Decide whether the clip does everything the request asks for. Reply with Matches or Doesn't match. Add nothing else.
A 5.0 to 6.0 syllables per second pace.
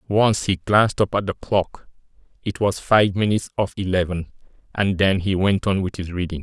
Matches